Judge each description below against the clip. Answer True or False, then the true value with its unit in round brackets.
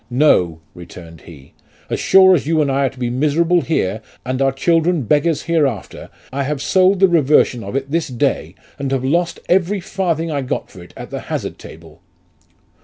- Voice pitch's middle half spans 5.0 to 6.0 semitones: True (5.3 semitones)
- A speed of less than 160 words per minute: False (200 wpm)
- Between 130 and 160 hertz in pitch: True (140 Hz)